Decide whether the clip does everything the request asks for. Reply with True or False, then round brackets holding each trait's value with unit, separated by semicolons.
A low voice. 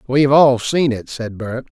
True (130 Hz)